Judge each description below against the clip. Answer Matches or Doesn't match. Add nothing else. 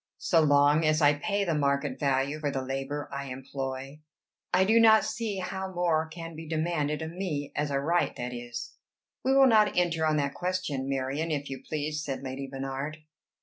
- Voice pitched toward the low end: Doesn't match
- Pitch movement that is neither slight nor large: Matches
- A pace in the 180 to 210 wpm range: Matches